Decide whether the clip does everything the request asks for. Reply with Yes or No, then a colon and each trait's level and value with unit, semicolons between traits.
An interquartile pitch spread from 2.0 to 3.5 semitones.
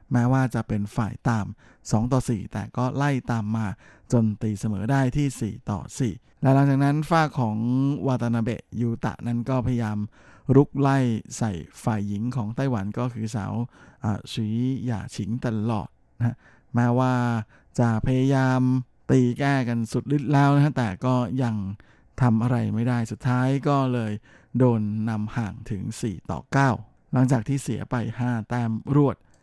Yes: average, 2.9 semitones